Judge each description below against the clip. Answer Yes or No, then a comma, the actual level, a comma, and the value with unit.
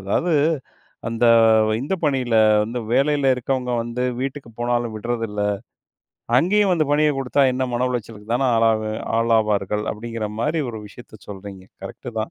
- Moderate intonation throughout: Yes, average, 3.7 semitones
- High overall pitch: No, low, 120 Hz